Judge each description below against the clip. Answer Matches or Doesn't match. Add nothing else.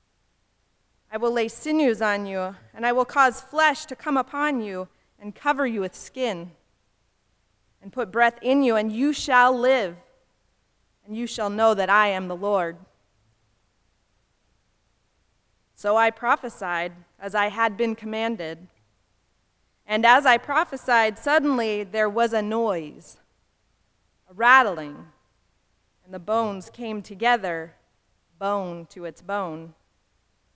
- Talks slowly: Matches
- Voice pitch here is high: Matches